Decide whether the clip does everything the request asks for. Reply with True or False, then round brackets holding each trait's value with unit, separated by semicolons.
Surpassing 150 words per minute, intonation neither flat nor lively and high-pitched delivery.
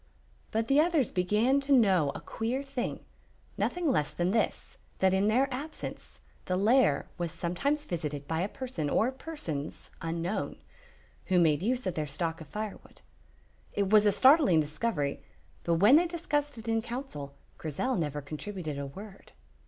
False (160 wpm; 8.0 semitones; 205 Hz)